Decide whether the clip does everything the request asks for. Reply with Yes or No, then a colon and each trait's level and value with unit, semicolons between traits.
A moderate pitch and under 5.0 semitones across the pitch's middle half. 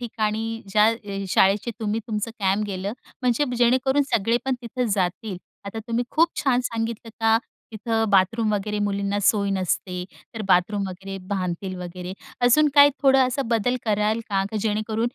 No: high, 215 Hz; average, 3.0 semitones